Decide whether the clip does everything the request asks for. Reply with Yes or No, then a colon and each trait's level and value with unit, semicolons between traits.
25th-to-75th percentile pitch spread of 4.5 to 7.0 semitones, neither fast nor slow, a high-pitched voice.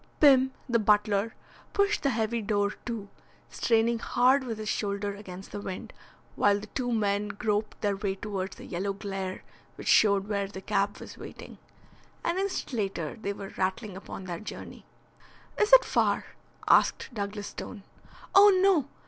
No: average, 2.9 semitones; average, 160 wpm; high, 210 Hz